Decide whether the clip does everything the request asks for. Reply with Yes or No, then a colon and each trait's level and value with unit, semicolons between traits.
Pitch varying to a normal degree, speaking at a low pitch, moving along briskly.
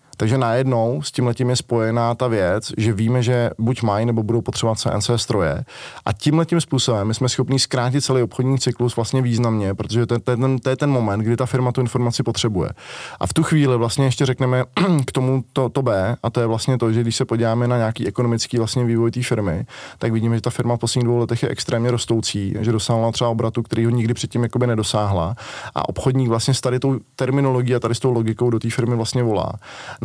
No: narrow, 2.1 semitones; low, 120 Hz; fast, 225 wpm